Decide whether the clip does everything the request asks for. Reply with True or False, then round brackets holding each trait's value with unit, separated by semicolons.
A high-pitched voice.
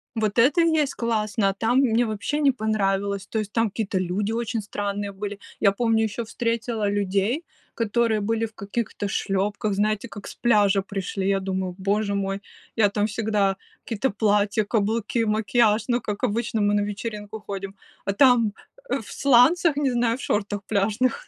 True (215 Hz)